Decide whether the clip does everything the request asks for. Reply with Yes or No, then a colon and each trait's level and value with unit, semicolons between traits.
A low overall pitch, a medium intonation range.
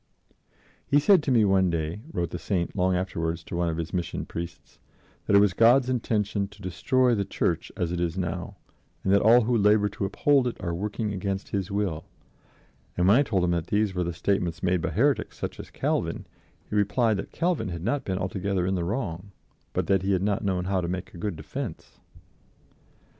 Yes: very low, 95 Hz; average, 3.2 semitones